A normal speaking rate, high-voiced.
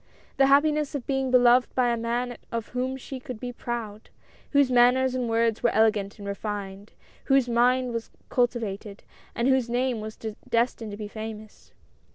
Yes: average, 175 wpm; high, 240 Hz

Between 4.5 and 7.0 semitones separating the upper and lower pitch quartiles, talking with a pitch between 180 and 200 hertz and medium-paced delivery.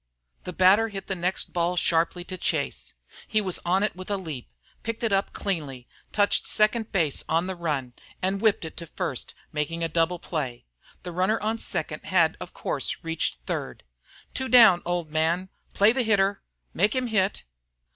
No: average, 3.8 semitones; medium, 185 Hz; average, 180 wpm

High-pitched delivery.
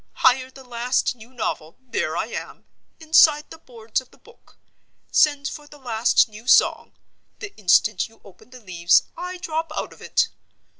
Yes: very high, 255 Hz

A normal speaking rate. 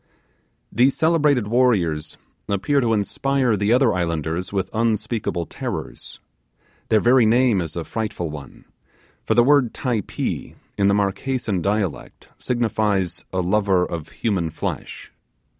No: slow, 125 wpm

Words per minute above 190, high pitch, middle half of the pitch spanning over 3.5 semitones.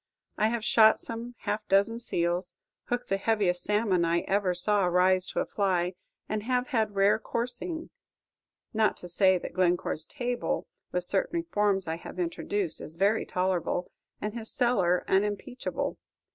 No: average, 155 wpm; high, 200 Hz; average, 3.9 semitones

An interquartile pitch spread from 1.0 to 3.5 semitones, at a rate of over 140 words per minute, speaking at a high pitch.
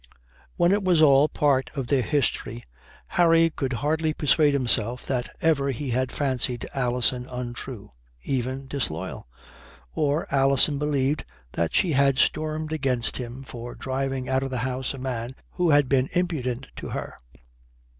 No: average, 2.9 semitones; average, 150 wpm; low, 135 Hz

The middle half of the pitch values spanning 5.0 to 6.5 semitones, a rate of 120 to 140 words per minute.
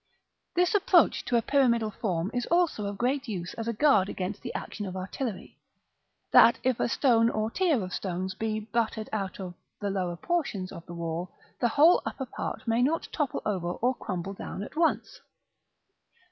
No: wide, 5.6 semitones; average, 185 wpm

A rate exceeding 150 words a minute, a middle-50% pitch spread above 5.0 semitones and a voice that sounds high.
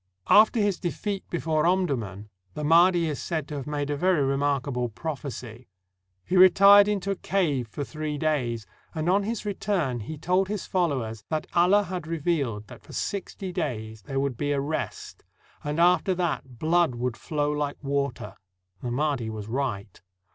No: average, 170 wpm; wide, 5.6 semitones; medium, 150 Hz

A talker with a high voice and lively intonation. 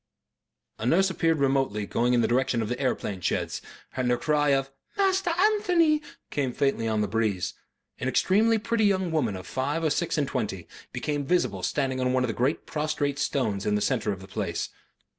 No: low, 135 Hz; wide, 6.4 semitones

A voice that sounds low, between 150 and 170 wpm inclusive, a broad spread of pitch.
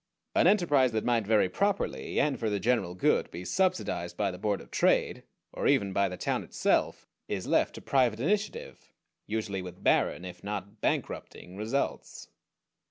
Yes: low, 110 Hz; average, 165 wpm; wide, 6.2 semitones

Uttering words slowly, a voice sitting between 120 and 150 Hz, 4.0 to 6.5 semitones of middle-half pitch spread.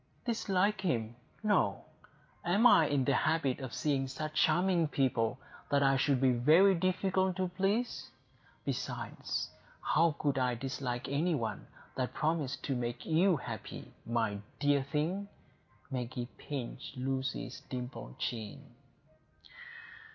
Yes: slow, 125 wpm; medium, 140 Hz; wide, 5.6 semitones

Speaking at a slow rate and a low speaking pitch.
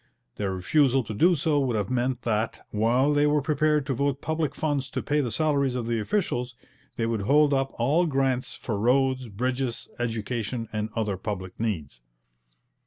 No: average, 175 wpm; low, 125 Hz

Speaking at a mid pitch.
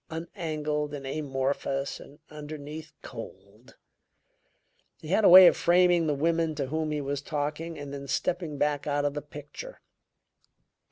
Yes: medium, 150 Hz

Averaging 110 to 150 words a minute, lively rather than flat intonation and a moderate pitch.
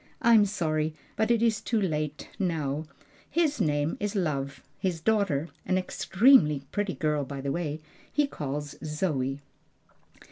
Yes: average, 140 wpm; wide, 5.9 semitones; medium, 160 Hz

